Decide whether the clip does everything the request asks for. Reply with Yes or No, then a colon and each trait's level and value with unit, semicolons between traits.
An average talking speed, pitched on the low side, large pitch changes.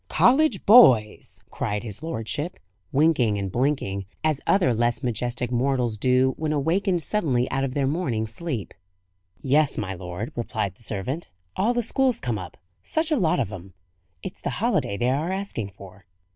Yes: average, 165 wpm; low, 130 Hz; wide, 7.1 semitones